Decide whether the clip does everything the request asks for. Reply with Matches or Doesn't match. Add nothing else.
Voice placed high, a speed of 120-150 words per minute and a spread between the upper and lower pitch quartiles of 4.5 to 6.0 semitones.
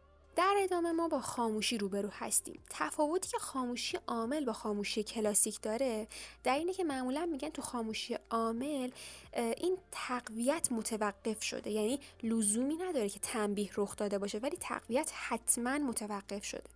Matches